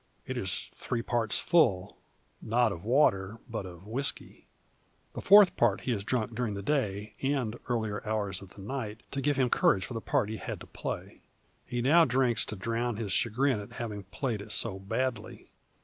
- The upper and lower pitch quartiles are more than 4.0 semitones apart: No, average, 3.7 semitones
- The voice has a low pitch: Yes, low, 115 Hz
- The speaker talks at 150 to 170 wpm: No, average, 190 wpm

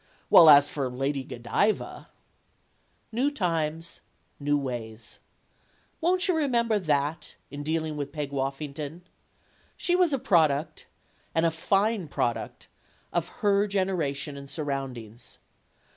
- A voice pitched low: No, medium, 155 Hz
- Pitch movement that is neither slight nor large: No, wide, 6.0 semitones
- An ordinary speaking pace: No, slow, 125 wpm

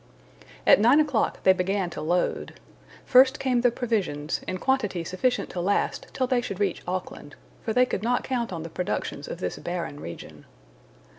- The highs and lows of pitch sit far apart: Yes, wide, 5.8 semitones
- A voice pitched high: Yes, high, 205 Hz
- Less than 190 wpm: Yes, average, 175 wpm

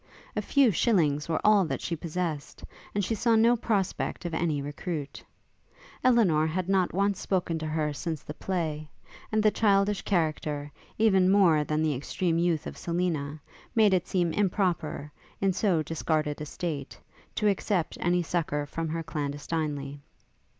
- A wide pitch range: No, average, 4.1 semitones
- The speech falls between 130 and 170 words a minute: Yes, average, 155 wpm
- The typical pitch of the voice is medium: Yes, medium, 170 Hz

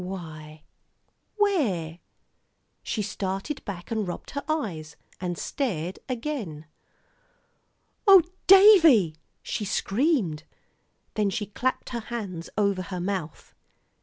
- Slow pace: Yes, slow, 105 wpm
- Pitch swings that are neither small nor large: No, wide, 7.0 semitones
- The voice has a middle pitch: No, high, 200 Hz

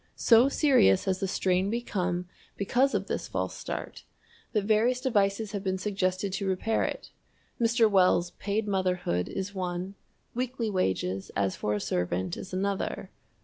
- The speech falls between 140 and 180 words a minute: Yes, average, 150 wpm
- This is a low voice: No, high, 195 Hz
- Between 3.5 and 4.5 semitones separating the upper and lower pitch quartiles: No, average, 3.1 semitones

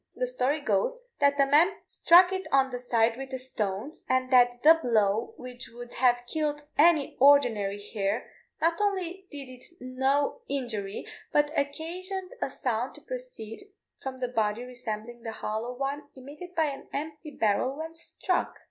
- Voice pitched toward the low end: No, very high, 265 Hz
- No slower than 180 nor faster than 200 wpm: No, average, 165 wpm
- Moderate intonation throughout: Yes, average, 4.5 semitones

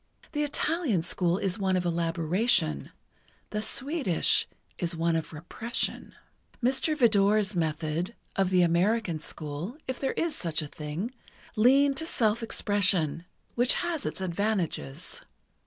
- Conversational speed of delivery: No, slow, 125 wpm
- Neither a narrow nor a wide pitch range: No, wide, 6.2 semitones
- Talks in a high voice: Yes, high, 195 Hz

